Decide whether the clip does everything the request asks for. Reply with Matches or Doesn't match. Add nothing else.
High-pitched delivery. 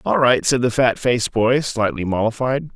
Doesn't match